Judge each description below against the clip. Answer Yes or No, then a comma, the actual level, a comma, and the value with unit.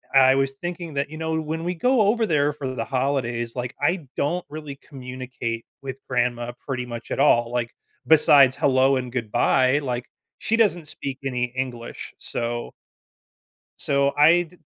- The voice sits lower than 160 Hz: Yes, low, 135 Hz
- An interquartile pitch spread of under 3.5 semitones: No, average, 3.9 semitones